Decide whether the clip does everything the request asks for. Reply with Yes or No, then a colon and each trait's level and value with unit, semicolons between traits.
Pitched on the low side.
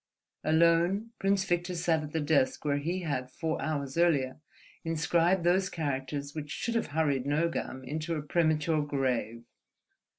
No: medium, 155 Hz